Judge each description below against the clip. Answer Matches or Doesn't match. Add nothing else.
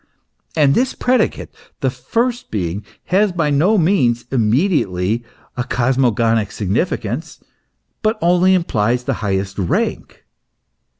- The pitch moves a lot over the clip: Matches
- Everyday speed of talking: Doesn't match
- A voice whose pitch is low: Matches